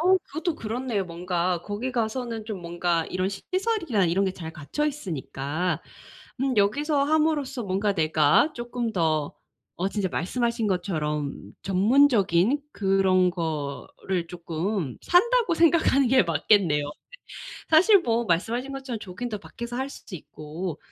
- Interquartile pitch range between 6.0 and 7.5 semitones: Yes, wide, 7.2 semitones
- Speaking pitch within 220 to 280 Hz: No, high, 200 Hz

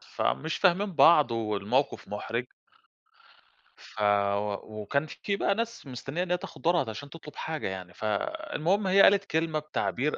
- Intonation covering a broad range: Yes, wide, 8.5 semitones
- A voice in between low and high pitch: Yes, medium, 150 Hz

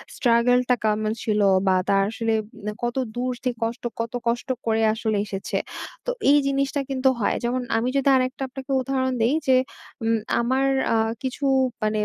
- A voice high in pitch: Yes, high, 240 Hz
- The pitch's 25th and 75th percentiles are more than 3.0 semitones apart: No, average, 2.7 semitones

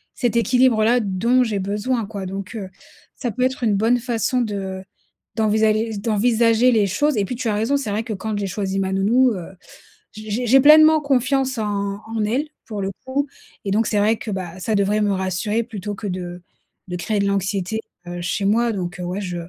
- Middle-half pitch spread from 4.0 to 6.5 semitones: No, average, 3.5 semitones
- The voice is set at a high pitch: Yes, high, 215 Hz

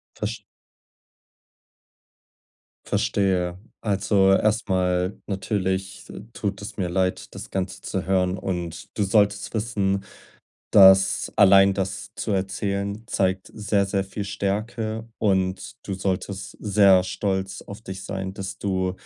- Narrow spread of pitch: Yes, narrow, 1.3 semitones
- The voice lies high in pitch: No, very low, 95 Hz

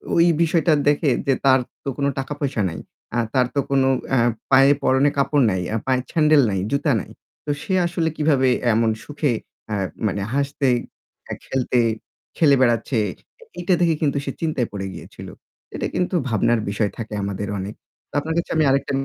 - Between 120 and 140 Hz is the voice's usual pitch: Yes, low, 135 Hz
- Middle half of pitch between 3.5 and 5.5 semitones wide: Yes, average, 4.2 semitones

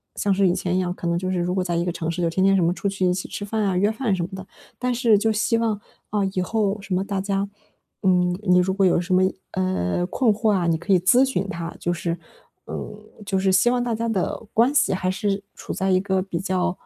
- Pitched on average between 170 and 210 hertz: Yes, high, 190 Hz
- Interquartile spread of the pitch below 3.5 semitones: Yes, narrow, 2.5 semitones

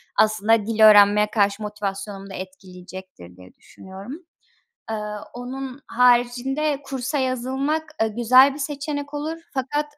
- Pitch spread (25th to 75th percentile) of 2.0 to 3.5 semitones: No, average, 5.1 semitones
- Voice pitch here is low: No, high, 240 Hz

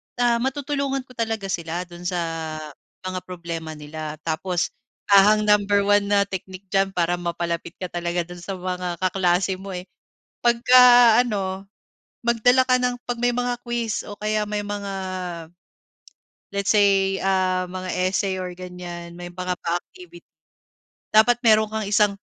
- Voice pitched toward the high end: Yes, high, 195 Hz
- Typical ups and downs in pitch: Yes, average, 3.8 semitones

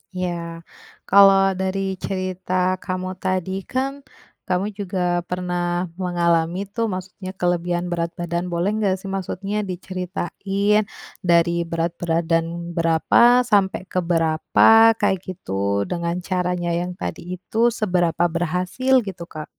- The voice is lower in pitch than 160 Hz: No, medium, 180 Hz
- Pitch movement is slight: Yes, narrow, 1.8 semitones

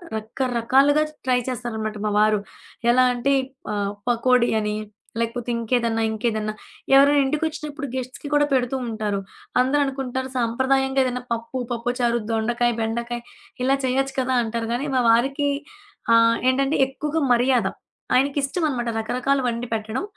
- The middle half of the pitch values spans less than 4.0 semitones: Yes, average, 2.7 semitones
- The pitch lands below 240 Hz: No, high, 245 Hz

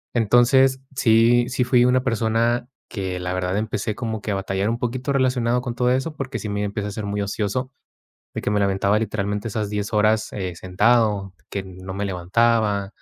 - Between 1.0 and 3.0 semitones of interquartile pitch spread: No, average, 3.4 semitones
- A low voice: Yes, low, 110 Hz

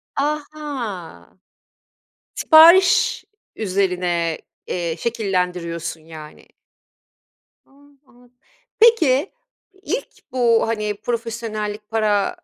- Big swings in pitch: Yes, wide, 7.2 semitones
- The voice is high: Yes, high, 220 Hz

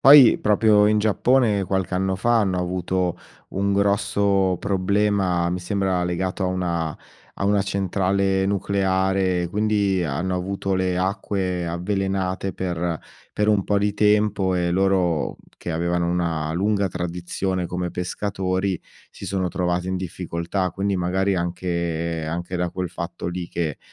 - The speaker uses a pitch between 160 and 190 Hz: No, very low, 95 Hz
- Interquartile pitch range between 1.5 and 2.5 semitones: Yes, narrow, 2.1 semitones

